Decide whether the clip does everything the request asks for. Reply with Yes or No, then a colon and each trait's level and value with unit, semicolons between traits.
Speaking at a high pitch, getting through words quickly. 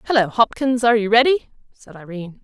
No: high, 225 Hz; average, 170 wpm